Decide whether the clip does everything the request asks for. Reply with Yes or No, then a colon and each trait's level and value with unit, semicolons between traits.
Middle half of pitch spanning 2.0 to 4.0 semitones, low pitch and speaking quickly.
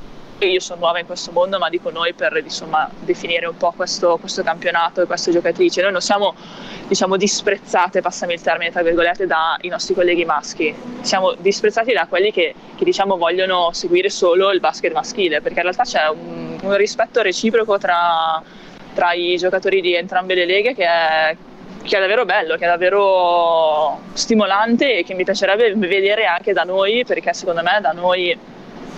No: average, 3.0 semitones; medium, 185 Hz; fast, 180 wpm